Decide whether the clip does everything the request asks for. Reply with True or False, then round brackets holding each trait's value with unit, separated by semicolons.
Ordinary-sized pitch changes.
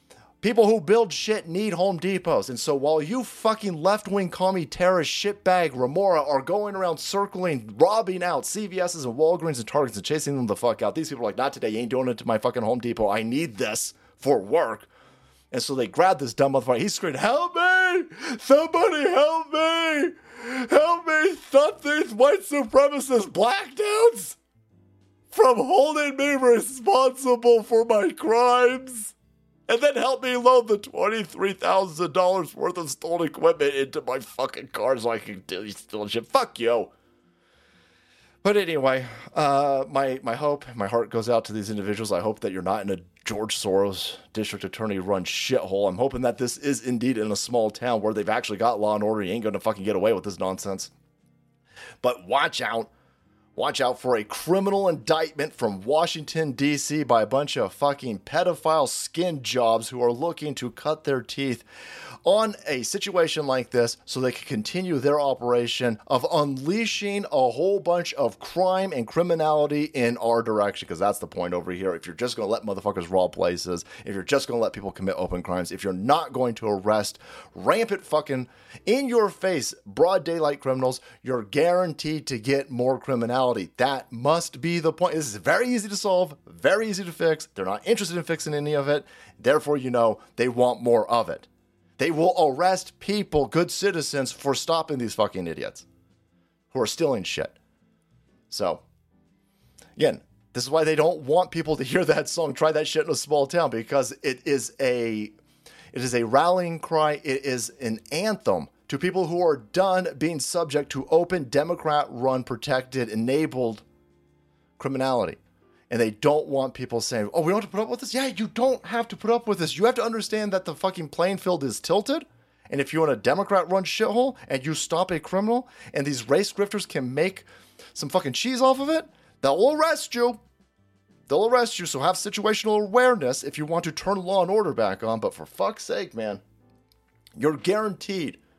False (8.5 semitones)